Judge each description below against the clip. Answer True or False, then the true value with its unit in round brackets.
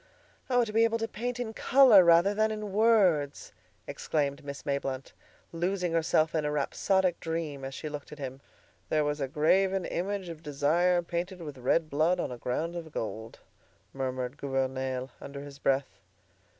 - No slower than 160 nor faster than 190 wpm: True (170 wpm)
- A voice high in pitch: False (160 Hz)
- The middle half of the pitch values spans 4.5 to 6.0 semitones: True (5.2 semitones)